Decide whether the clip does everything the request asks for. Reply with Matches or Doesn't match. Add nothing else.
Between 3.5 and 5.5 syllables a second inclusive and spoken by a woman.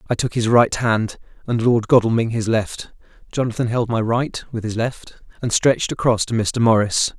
Doesn't match